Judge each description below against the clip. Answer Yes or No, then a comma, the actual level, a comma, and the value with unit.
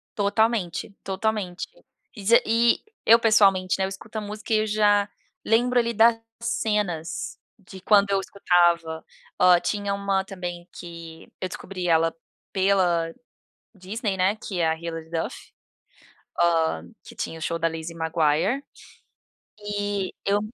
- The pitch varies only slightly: No, average, 3.8 semitones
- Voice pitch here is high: Yes, high, 195 Hz